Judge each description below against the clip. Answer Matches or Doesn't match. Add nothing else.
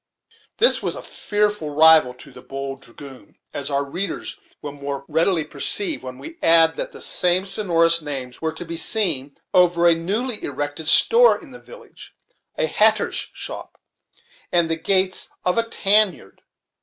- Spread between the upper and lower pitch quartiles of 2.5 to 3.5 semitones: Doesn't match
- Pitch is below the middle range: Doesn't match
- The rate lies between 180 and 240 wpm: Doesn't match